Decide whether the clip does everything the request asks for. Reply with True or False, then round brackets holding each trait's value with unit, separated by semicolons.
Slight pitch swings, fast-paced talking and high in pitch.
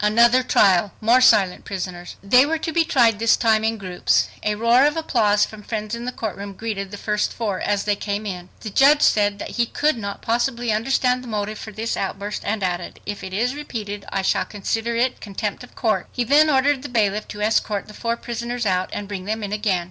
False (3.0 semitones; 225 wpm; 215 Hz)